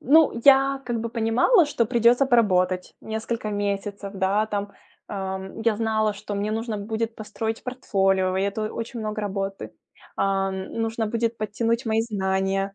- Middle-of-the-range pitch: No, high, 215 Hz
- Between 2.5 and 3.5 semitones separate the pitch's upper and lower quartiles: Yes, average, 2.8 semitones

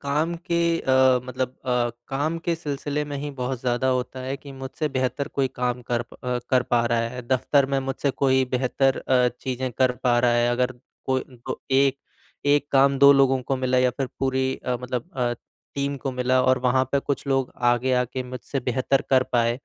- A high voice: No, low, 130 Hz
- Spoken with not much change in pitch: Yes, narrow, 1.6 semitones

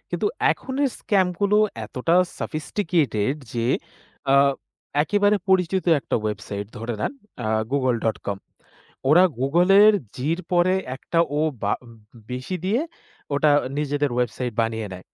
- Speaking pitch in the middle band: Yes, medium, 150 Hz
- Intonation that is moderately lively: No, wide, 7.6 semitones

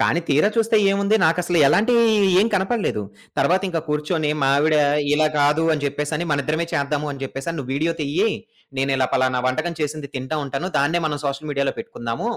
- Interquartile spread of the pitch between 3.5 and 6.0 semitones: Yes, average, 3.8 semitones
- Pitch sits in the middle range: Yes, medium, 150 Hz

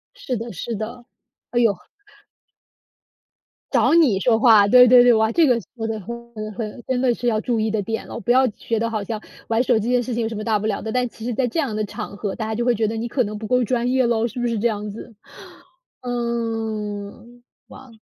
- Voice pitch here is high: Yes, high, 230 Hz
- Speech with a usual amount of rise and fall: No, narrow, 2.1 semitones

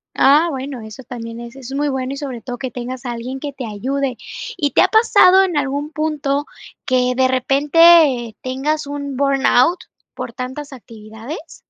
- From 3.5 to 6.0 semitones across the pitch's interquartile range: No, narrow, 2.6 semitones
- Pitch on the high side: Yes, very high, 270 Hz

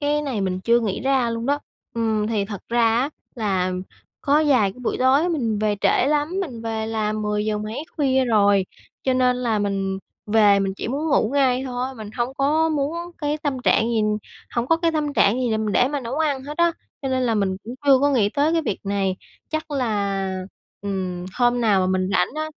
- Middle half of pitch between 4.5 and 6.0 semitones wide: Yes, average, 5.2 semitones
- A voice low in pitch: No, high, 235 Hz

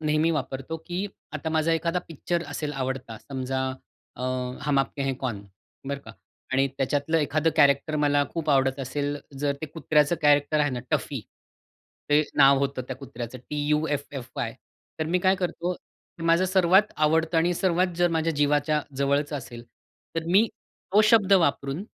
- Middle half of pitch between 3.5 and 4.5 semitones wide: No, average, 3.1 semitones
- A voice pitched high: No, medium, 150 Hz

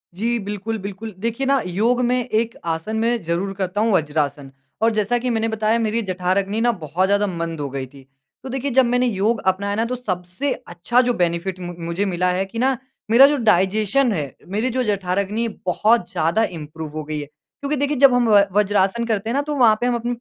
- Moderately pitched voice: No, high, 210 Hz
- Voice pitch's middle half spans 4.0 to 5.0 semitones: Yes, average, 4.7 semitones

